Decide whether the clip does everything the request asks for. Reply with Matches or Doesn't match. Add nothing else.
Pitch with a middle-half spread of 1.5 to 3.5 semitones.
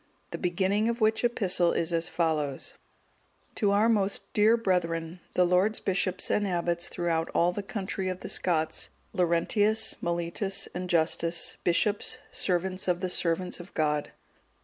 Matches